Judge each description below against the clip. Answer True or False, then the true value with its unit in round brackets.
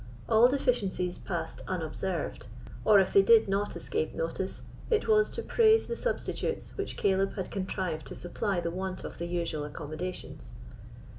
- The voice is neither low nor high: False (195 Hz)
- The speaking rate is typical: True (155 wpm)